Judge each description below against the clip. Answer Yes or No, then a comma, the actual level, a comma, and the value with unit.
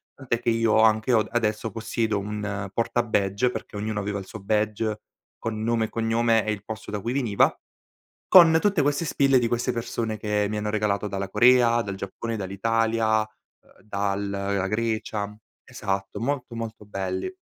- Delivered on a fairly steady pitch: Yes, narrow, 2.3 semitones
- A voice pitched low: Yes, low, 110 Hz